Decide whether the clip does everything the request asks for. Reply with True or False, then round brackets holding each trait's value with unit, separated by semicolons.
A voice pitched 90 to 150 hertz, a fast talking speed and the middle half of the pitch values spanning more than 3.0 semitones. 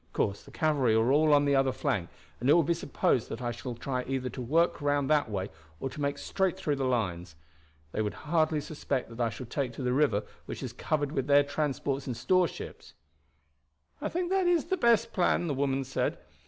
True (140 Hz; 225 wpm; 3.7 semitones)